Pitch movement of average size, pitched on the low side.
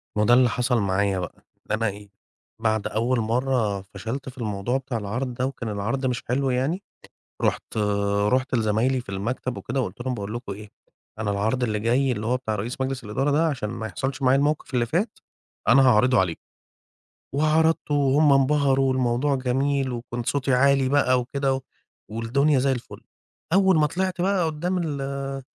Yes: average, 3.5 semitones; low, 130 Hz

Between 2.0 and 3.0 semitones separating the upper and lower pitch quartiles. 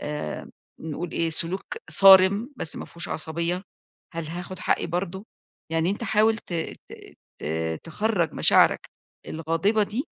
No: average, 3.5 semitones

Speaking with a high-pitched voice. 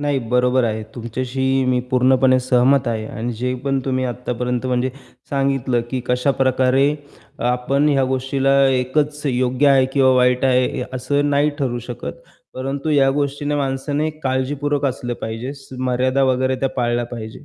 No: low, 130 Hz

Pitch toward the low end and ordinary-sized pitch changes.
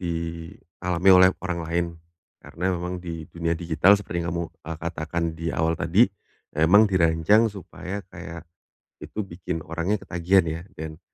No: very low, 85 Hz; narrow, 2.0 semitones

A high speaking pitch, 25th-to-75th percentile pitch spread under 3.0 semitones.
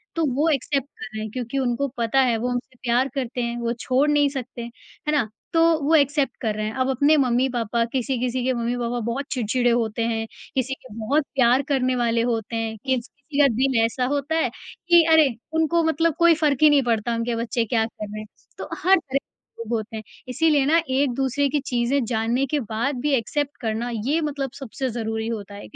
No: very high, 255 Hz; average, 3.4 semitones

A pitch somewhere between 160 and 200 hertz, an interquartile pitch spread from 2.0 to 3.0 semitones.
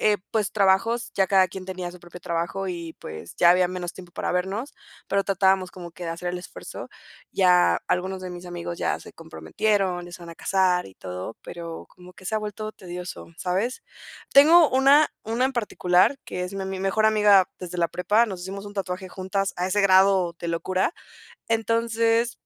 Yes: medium, 185 Hz; average, 2.7 semitones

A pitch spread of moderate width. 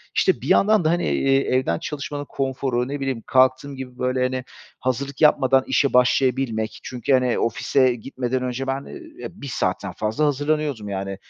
No: narrow, 1.9 semitones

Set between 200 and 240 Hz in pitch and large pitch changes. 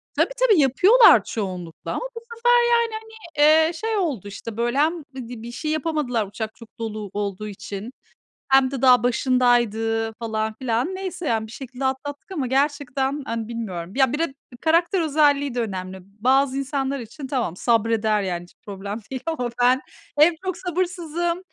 No: very high, 260 Hz; wide, 5.8 semitones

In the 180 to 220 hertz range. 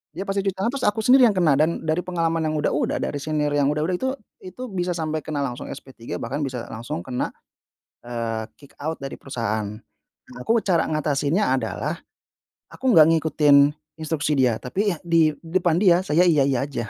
No: medium, 155 Hz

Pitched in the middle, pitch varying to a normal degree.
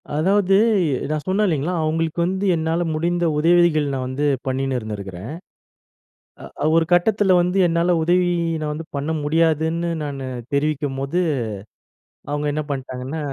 Yes: medium, 155 Hz; average, 3.6 semitones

